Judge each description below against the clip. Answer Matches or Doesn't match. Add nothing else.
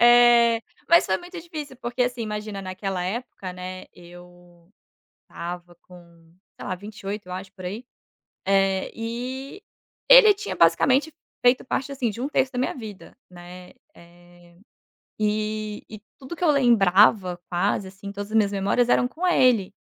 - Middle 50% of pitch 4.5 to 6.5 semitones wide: Matches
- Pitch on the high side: Matches